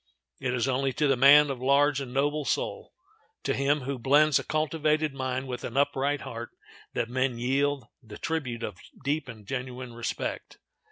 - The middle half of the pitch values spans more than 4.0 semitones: No, narrow, 2.6 semitones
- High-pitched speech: No, low, 135 Hz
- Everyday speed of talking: Yes, average, 165 wpm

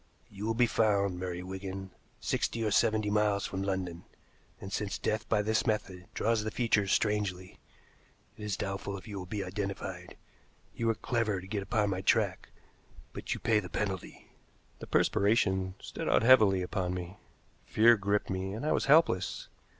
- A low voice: Yes, low, 100 Hz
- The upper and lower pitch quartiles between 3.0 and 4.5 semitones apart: No, narrow, 2.4 semitones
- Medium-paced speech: Yes, average, 175 wpm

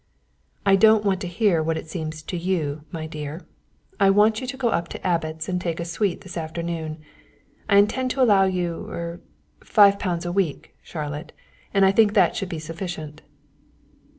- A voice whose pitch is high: No, medium, 175 Hz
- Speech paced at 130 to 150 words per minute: No, average, 180 wpm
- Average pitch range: Yes, average, 3.7 semitones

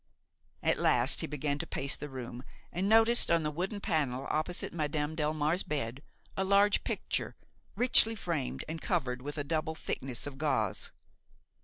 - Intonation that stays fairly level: No, average, 4.0 semitones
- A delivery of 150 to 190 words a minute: Yes, average, 160 wpm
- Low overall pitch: No, medium, 155 Hz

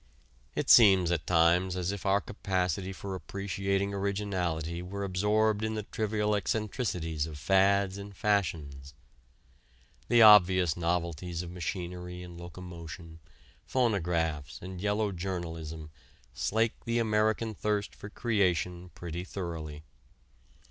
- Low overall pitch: Yes, very low, 95 Hz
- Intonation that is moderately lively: Yes, average, 3.1 semitones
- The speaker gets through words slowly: Yes, slow, 115 wpm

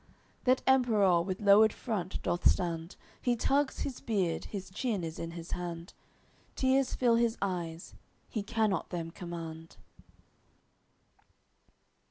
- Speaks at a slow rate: Yes, slow, 125 wpm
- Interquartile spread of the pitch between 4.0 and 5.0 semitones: No, wide, 5.4 semitones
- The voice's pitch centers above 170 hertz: Yes, high, 190 Hz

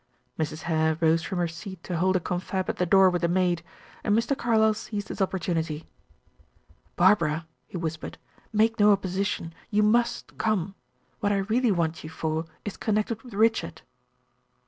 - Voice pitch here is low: No, high, 190 Hz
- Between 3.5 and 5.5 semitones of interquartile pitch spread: Yes, average, 4.3 semitones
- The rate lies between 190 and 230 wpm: No, average, 170 wpm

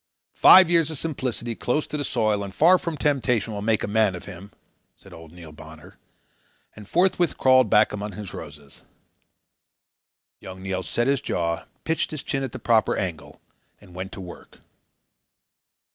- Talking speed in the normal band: Yes, average, 170 wpm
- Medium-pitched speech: No, low, 105 Hz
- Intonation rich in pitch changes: Yes, wide, 6.8 semitones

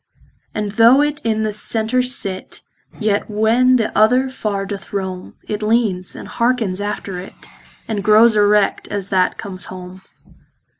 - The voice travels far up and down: No, average, 2.8 semitones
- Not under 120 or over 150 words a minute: Yes, average, 145 wpm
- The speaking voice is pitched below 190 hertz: No, high, 210 Hz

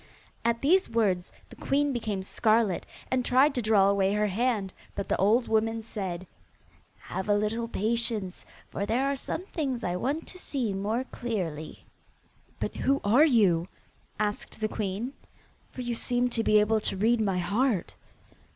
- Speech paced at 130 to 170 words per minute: Yes, average, 165 wpm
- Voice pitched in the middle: No, high, 220 Hz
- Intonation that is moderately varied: Yes, average, 3.7 semitones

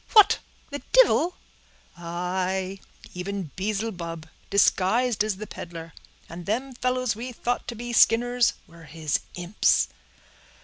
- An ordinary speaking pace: No, slow, 120 wpm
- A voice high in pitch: Yes, high, 200 Hz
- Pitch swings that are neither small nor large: No, wide, 5.7 semitones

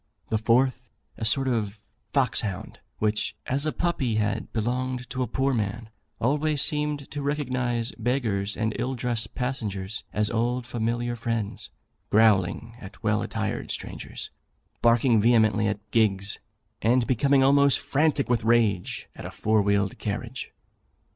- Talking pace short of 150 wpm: Yes, average, 140 wpm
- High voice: No, low, 115 Hz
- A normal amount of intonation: Yes, average, 3.1 semitones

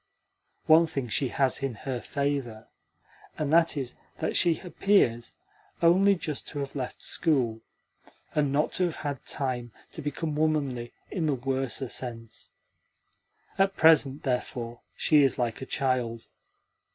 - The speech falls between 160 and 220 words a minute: No, average, 140 wpm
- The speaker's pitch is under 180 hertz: Yes, low, 135 Hz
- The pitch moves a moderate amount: Yes, average, 4.1 semitones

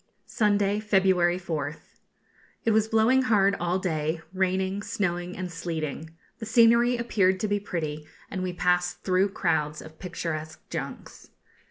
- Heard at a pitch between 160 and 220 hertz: Yes, medium, 185 Hz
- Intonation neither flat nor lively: Yes, average, 3.7 semitones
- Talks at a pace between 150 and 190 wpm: No, average, 140 wpm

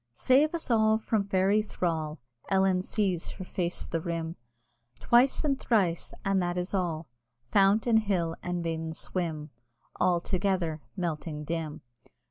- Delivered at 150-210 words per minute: No, average, 140 wpm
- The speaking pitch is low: No, medium, 180 Hz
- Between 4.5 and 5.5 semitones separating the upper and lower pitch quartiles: No, average, 3.8 semitones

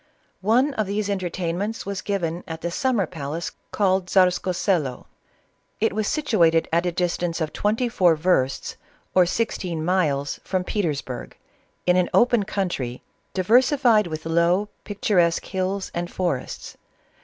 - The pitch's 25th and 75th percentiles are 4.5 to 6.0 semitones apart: No, average, 3.5 semitones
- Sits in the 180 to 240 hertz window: Yes, medium, 185 Hz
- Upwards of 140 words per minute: No, slow, 135 wpm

